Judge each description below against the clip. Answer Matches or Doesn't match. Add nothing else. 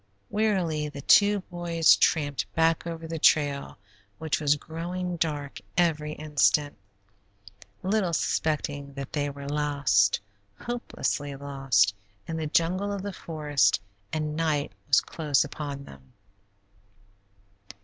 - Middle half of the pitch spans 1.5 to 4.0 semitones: Matches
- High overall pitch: Doesn't match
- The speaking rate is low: Matches